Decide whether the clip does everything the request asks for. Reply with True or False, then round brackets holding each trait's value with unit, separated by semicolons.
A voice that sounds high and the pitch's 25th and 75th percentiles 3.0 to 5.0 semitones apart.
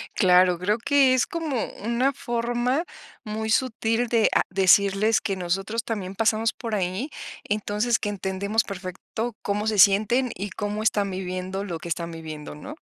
True (210 Hz; 3.6 semitones)